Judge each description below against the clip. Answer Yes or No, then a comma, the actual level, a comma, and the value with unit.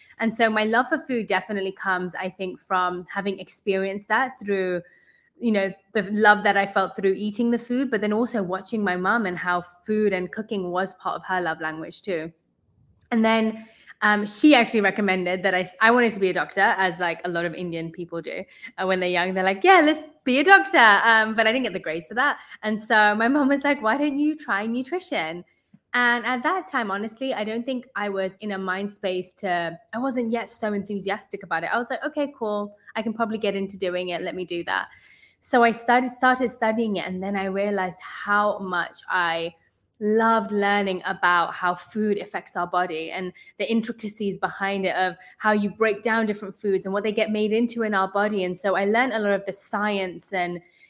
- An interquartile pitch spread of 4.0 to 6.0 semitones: No, average, 3.4 semitones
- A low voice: No, high, 205 Hz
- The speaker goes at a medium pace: No, fast, 220 wpm